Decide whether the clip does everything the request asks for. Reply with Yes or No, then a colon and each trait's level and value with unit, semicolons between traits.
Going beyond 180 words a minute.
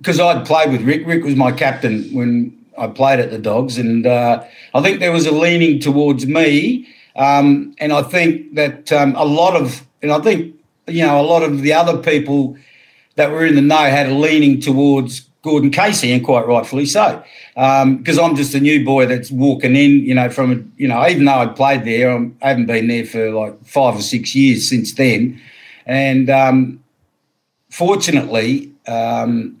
Yes: average, 195 wpm